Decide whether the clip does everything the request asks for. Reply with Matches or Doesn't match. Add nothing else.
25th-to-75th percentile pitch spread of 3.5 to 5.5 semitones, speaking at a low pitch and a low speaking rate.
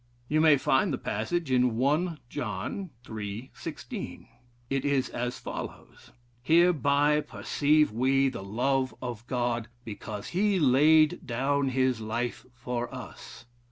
Matches